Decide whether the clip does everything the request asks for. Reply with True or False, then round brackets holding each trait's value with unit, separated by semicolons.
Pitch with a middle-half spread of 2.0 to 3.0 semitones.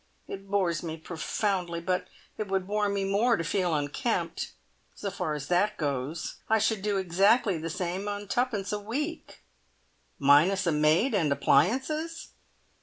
False (3.9 semitones)